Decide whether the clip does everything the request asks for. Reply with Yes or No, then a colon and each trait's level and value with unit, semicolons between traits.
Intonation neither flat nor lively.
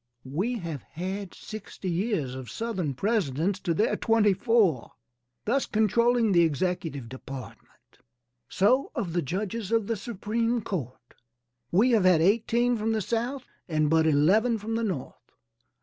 No: wide, 5.9 semitones